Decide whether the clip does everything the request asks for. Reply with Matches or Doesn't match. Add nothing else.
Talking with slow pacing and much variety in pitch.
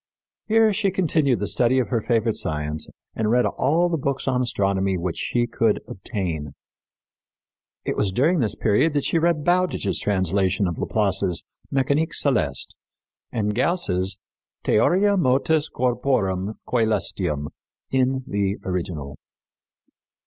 Matches